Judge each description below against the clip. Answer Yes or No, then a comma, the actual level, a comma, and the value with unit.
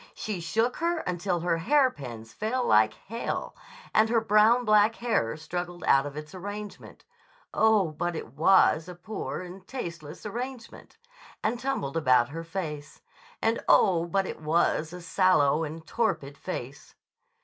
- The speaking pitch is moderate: Yes, medium, 180 Hz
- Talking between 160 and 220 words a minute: No, average, 150 wpm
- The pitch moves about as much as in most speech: No, wide, 5.9 semitones